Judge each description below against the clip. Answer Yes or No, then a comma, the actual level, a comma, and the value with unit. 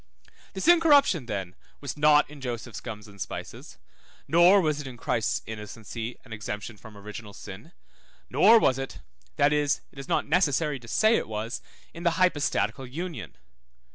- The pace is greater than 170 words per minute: No, average, 165 wpm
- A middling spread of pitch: No, wide, 6.6 semitones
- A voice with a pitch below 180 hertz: Yes, low, 135 Hz